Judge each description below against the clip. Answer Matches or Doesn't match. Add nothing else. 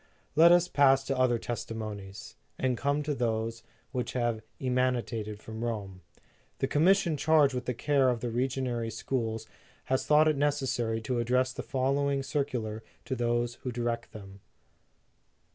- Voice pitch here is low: Matches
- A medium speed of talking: Matches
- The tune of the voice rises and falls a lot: Doesn't match